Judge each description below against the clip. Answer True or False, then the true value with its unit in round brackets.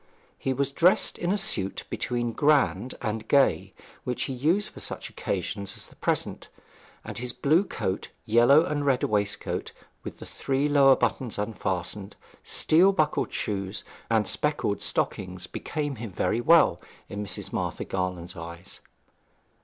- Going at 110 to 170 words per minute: True (145 wpm)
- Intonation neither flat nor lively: False (6.5 semitones)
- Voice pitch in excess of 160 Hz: False (120 Hz)